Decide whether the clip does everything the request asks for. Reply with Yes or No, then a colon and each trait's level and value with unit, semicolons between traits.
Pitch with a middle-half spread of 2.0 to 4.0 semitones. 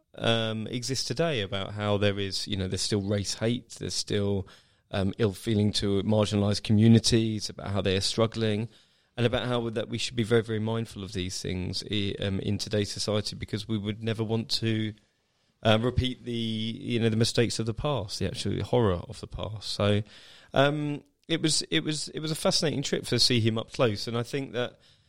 Yes: average, 2.8 semitones